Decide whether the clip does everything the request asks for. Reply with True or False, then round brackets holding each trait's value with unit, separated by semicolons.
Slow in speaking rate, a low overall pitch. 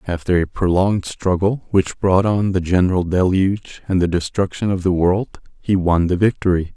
False (180 wpm; 95 Hz)